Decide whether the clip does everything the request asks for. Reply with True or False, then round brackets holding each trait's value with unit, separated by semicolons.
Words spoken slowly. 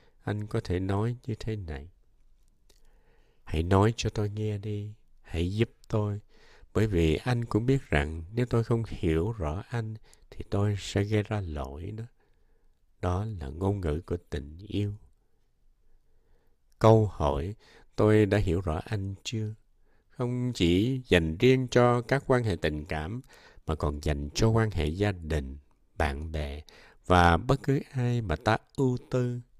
True (160 wpm)